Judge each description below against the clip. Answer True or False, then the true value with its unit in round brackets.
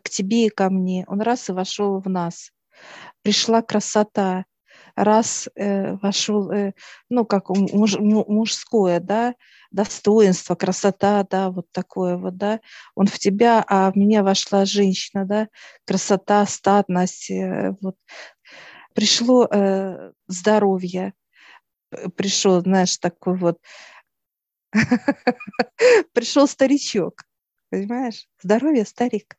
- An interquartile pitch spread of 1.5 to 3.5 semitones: True (2.6 semitones)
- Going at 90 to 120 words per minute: True (110 wpm)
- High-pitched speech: True (200 Hz)